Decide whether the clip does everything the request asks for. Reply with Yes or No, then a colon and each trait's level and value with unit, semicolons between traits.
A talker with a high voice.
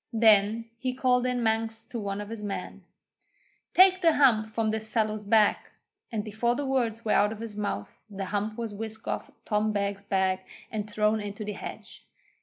Yes: high, 215 Hz